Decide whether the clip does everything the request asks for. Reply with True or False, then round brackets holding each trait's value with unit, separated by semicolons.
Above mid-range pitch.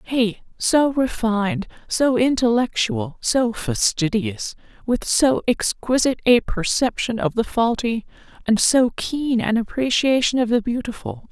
True (235 Hz)